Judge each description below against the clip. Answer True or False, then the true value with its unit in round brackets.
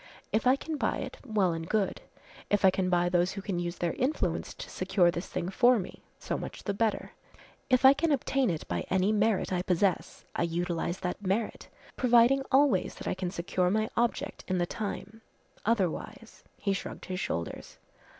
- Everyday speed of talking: True (195 wpm)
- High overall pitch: True (195 Hz)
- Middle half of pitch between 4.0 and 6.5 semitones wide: True (4.6 semitones)